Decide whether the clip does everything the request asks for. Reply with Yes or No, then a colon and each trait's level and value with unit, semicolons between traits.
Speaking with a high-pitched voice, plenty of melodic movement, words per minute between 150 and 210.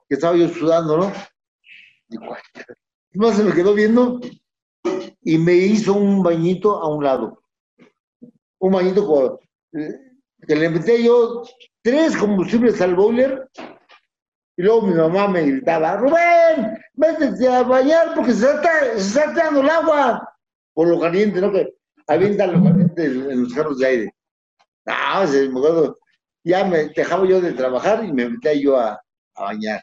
Yes: high, 200 Hz; wide, 6.8 semitones; average, 155 wpm